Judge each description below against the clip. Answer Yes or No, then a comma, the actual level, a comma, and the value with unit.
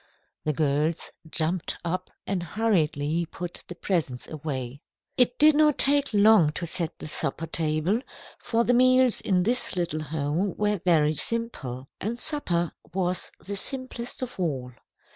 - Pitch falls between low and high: Yes, medium, 175 Hz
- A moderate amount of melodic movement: No, wide, 6.7 semitones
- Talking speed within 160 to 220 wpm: No, average, 145 wpm